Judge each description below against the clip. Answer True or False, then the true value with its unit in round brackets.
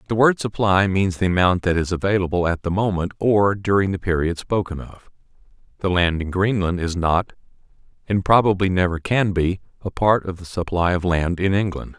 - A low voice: True (95 Hz)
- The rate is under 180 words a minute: False (190 wpm)